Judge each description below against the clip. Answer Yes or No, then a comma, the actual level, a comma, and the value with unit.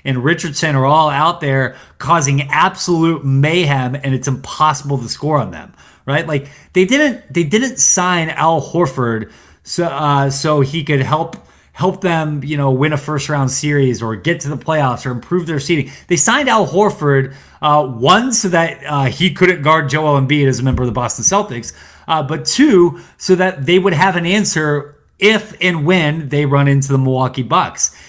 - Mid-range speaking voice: Yes, medium, 150 Hz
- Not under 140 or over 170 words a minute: No, average, 190 wpm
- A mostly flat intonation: No, average, 4.2 semitones